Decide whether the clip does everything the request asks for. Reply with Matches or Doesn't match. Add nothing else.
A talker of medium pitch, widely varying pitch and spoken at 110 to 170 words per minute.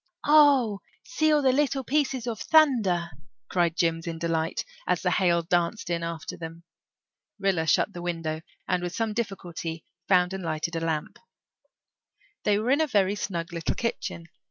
Matches